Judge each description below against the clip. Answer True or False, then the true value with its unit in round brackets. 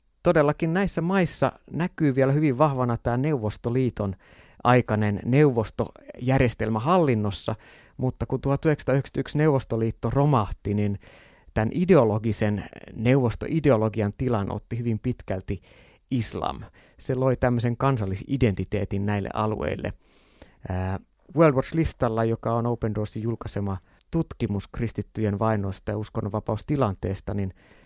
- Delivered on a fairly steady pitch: False (4.6 semitones)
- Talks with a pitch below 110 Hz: False (115 Hz)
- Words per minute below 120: True (95 wpm)